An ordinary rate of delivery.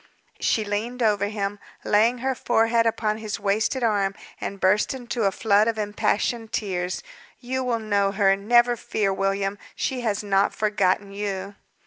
Yes: average, 155 wpm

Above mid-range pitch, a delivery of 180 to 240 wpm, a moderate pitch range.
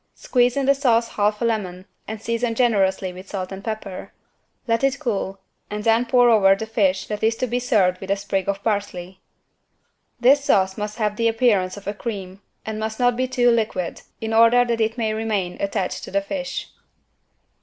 Yes: high, 220 Hz; average, 195 wpm; average, 3.2 semitones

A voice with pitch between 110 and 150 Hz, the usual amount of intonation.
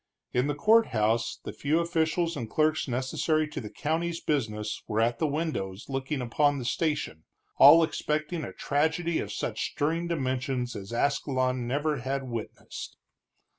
Yes: medium, 140 Hz; average, 4.4 semitones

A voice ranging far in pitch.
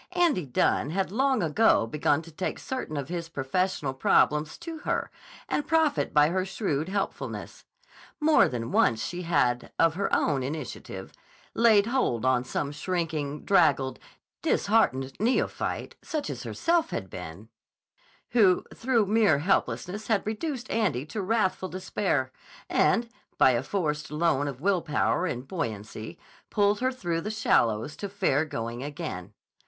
Yes: wide, 7.5 semitones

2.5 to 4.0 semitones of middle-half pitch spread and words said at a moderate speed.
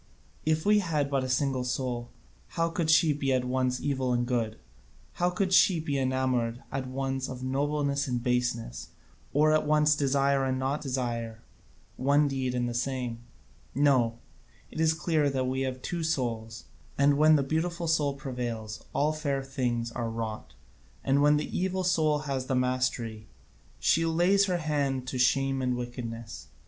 Yes: average, 3.3 semitones; average, 170 wpm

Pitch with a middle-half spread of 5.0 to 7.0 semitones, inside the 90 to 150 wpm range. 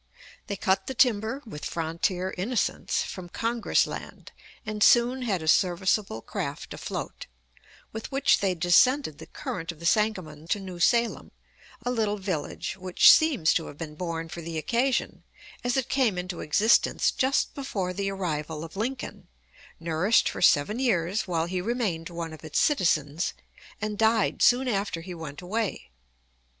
No: wide, 5.5 semitones; average, 160 wpm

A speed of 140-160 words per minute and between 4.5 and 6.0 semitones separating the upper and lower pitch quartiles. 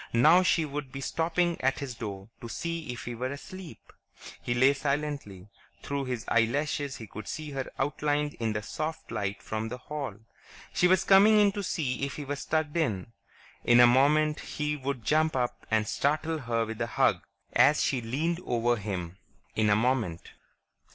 No: average, 185 wpm; average, 4.8 semitones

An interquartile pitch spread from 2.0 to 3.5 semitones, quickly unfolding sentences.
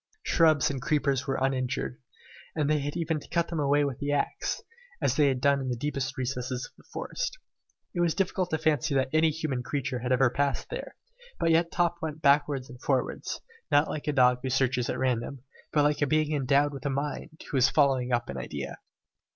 Yes: average, 2.9 semitones; fast, 215 wpm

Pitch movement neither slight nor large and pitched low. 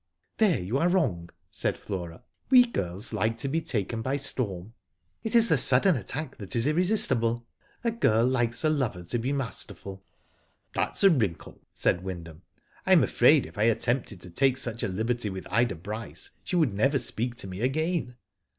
No: wide, 6.3 semitones; low, 120 Hz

